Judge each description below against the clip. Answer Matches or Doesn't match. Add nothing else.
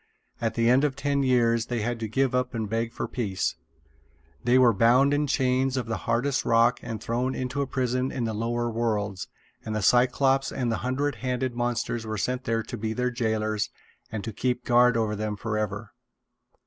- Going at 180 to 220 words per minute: Matches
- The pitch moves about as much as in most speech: Doesn't match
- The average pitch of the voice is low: Matches